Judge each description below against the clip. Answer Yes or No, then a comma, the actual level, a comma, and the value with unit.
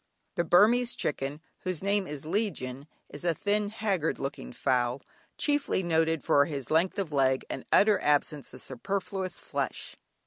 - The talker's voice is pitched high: No, medium, 165 Hz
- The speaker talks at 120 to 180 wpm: Yes, average, 150 wpm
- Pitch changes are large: Yes, wide, 6.1 semitones